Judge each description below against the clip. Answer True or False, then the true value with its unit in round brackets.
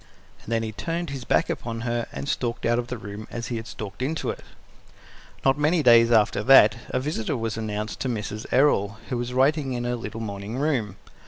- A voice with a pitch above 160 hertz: False (120 Hz)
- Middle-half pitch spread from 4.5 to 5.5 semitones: False (3.3 semitones)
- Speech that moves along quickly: True (215 wpm)